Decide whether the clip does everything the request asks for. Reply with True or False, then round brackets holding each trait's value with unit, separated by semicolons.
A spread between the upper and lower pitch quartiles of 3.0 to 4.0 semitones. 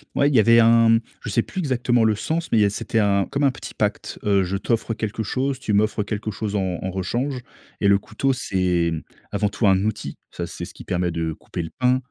True (3.7 semitones)